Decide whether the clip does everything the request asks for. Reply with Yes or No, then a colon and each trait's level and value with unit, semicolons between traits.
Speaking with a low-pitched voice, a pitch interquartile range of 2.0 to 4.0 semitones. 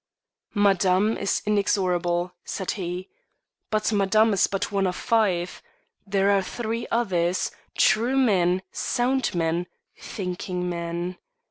No: high, 195 Hz; average, 3.1 semitones